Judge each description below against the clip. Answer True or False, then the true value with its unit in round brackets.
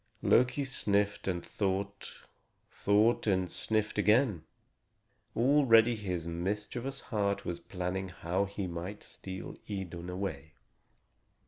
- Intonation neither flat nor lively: True (3.2 semitones)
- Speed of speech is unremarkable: False (105 wpm)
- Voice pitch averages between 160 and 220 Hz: False (100 Hz)